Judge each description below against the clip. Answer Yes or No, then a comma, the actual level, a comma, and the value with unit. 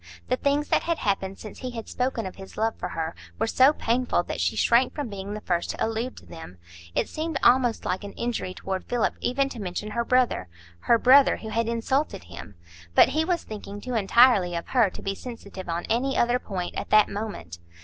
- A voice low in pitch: No, high, 225 Hz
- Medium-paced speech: No, fast, 215 wpm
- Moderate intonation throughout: Yes, average, 4.8 semitones